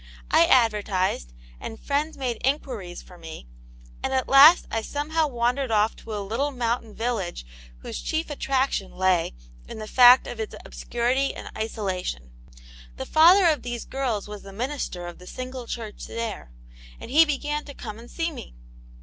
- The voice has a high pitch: Yes, high, 240 Hz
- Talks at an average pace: Yes, average, 165 wpm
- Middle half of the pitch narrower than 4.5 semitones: No, average, 4.9 semitones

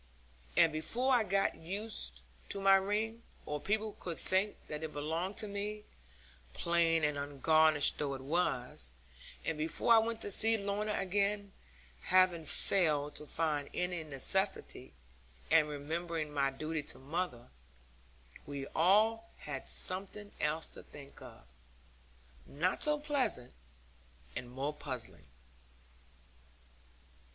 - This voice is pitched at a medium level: Yes, medium, 165 Hz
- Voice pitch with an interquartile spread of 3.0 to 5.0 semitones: No, wide, 5.4 semitones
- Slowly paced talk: Yes, slow, 125 wpm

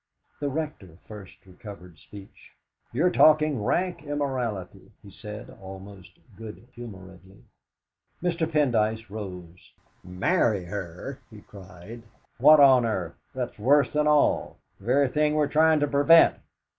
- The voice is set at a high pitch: No, low, 115 Hz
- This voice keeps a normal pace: No, slow, 125 wpm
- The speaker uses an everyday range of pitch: No, wide, 7.2 semitones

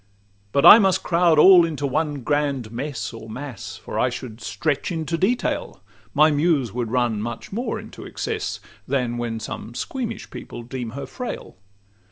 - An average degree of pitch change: No, wide, 5.9 semitones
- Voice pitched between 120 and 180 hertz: Yes, medium, 140 Hz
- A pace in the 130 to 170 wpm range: Yes, average, 165 wpm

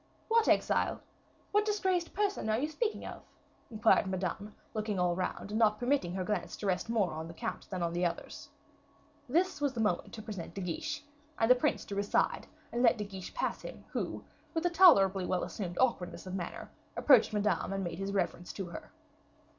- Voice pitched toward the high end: Yes, high, 210 Hz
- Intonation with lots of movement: Yes, wide, 6.0 semitones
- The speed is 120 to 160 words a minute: No, average, 200 wpm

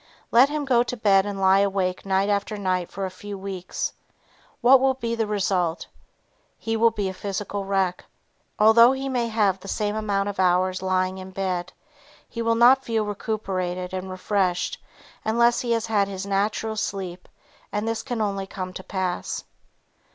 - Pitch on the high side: Yes, high, 200 Hz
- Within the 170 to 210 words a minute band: Yes, average, 175 wpm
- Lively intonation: No, average, 3.0 semitones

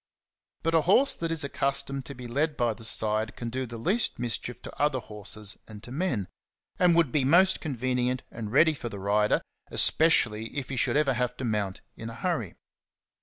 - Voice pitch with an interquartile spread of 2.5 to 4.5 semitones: No, average, 5.1 semitones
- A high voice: No, low, 125 Hz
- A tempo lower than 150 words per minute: No, average, 200 wpm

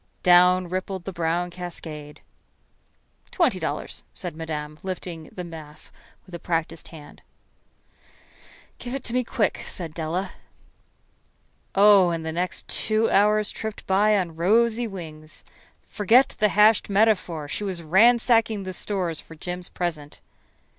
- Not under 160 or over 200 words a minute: No, slow, 135 wpm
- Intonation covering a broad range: No, average, 4.2 semitones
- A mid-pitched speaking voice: Yes, medium, 180 Hz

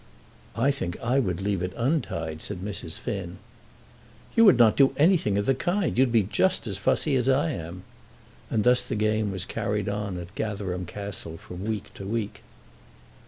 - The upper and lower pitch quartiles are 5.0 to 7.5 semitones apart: Yes, wide, 5.4 semitones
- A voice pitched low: Yes, low, 105 Hz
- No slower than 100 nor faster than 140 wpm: No, average, 180 wpm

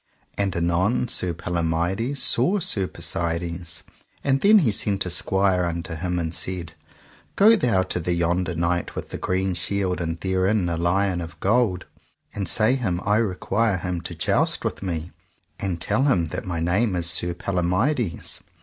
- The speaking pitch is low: Yes, very low, 90 Hz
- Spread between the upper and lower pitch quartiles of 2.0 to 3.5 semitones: Yes, average, 2.9 semitones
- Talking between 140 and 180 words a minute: Yes, average, 170 wpm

